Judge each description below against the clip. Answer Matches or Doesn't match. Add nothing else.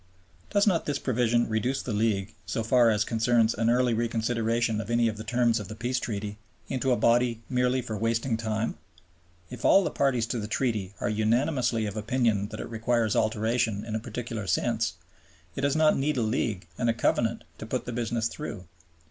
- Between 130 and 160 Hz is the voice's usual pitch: Doesn't match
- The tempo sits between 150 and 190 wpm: Doesn't match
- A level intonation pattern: Matches